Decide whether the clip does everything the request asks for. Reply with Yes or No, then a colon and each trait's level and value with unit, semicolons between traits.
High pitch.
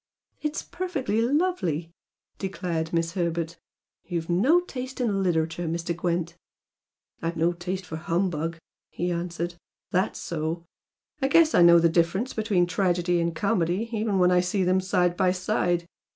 No: medium, 175 Hz